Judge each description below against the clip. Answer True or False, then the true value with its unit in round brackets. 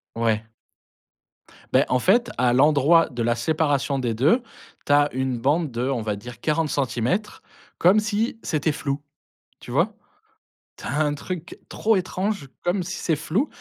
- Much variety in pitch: True (5.7 semitones)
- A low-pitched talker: False (145 Hz)